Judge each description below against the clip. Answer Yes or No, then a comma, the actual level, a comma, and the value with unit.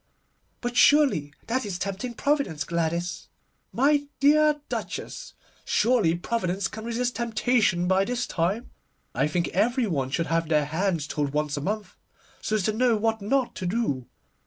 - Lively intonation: Yes, wide, 6.6 semitones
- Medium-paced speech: Yes, average, 160 wpm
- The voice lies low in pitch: No, high, 200 Hz